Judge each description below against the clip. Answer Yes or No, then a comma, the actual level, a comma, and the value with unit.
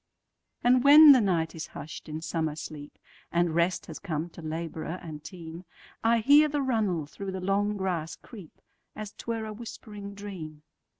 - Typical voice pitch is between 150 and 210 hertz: Yes, medium, 185 Hz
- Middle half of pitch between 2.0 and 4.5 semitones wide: No, average, 5.0 semitones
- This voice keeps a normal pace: Yes, average, 160 wpm